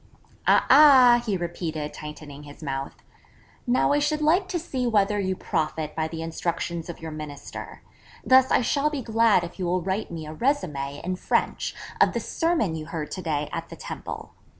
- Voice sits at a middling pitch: Yes, medium, 180 Hz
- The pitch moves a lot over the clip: Yes, wide, 8.1 semitones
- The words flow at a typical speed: Yes, average, 190 wpm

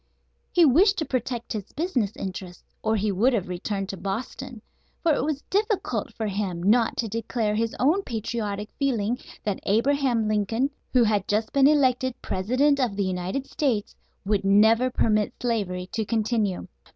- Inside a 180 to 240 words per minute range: No, average, 165 wpm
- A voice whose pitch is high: Yes, high, 225 Hz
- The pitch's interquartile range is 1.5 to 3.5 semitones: No, average, 4.2 semitones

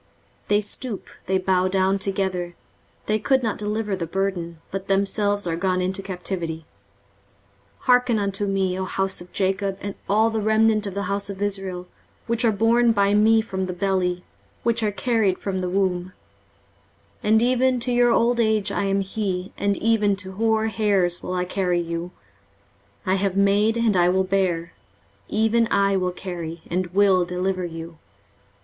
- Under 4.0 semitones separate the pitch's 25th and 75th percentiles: Yes, average, 2.8 semitones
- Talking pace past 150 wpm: Yes, average, 175 wpm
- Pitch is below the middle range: No, high, 195 Hz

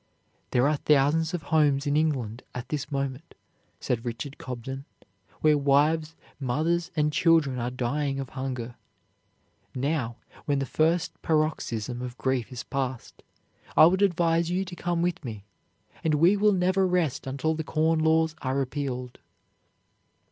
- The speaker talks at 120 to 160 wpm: Yes, average, 150 wpm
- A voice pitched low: No, medium, 145 Hz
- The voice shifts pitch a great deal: No, average, 3.8 semitones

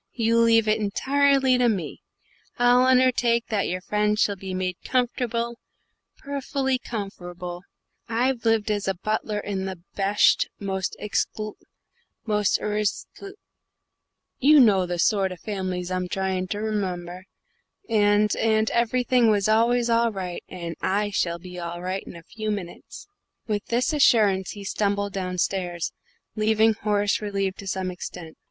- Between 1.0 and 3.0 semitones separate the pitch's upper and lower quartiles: No, average, 3.6 semitones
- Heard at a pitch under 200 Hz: No, high, 210 Hz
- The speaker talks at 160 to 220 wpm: No, average, 145 wpm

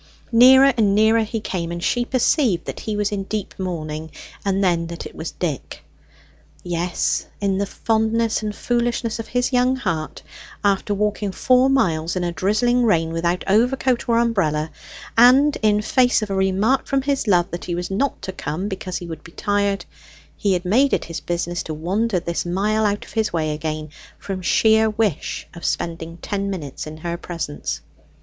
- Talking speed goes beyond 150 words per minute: Yes, average, 185 wpm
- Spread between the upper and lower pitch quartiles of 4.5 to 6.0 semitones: Yes, average, 4.8 semitones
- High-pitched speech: Yes, high, 200 Hz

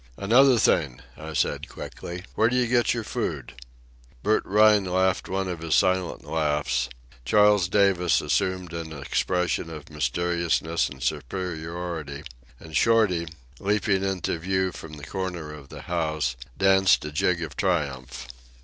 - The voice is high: No, very low, 90 Hz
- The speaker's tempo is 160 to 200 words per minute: No, average, 140 wpm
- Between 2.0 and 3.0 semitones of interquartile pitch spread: No, average, 3.7 semitones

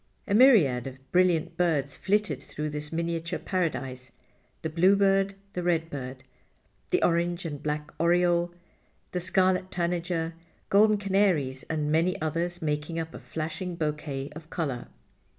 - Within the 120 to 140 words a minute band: Yes, slow, 135 wpm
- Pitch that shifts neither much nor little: Yes, average, 3.2 semitones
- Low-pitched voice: No, medium, 165 Hz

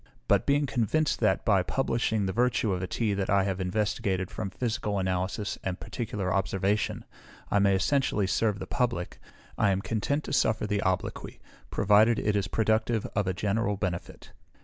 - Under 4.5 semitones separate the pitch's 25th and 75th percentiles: Yes, average, 2.7 semitones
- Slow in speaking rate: No, average, 170 wpm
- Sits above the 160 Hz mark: No, low, 105 Hz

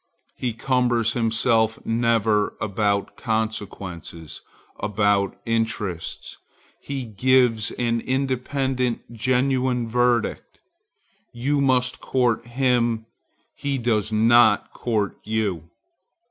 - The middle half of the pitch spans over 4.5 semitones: No, narrow, 2.6 semitones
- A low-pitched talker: Yes, low, 115 Hz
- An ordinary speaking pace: No, slow, 85 wpm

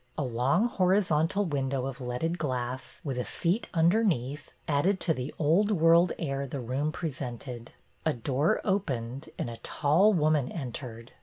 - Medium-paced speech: Yes, average, 160 wpm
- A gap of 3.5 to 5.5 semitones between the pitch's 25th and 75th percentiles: Yes, average, 5.0 semitones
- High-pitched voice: No, medium, 145 Hz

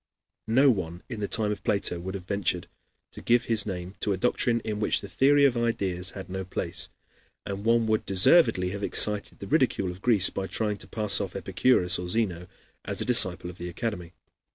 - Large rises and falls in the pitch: No, average, 3.8 semitones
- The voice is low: Yes, low, 100 Hz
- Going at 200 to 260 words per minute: Yes, fast, 205 wpm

